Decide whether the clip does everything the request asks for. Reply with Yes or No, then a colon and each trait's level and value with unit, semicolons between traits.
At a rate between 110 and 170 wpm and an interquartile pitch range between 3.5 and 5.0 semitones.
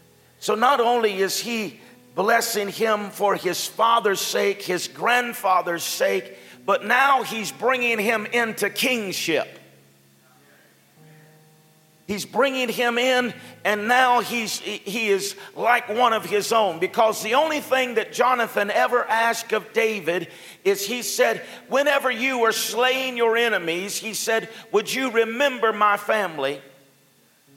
Yes: slow, 135 wpm; average, 4.7 semitones